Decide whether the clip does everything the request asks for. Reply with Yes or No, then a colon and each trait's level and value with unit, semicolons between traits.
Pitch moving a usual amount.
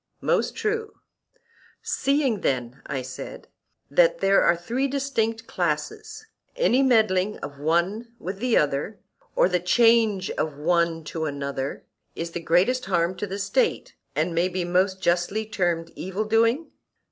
No: wide, 5.8 semitones